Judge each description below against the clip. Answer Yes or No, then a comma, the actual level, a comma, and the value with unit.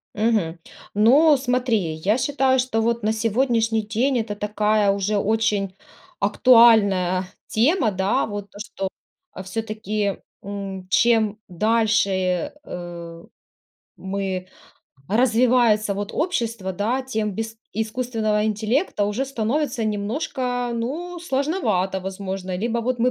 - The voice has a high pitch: Yes, high, 220 Hz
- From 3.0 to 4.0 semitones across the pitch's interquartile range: Yes, average, 3.4 semitones